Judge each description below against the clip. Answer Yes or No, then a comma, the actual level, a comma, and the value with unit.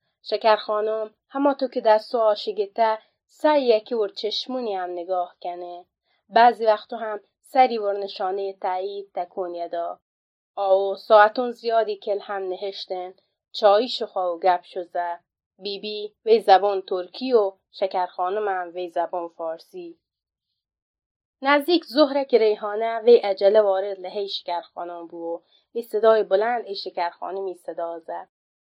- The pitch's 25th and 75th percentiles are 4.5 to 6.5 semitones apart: No, average, 3.6 semitones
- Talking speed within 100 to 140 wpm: Yes, average, 130 wpm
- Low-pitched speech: No, high, 200 Hz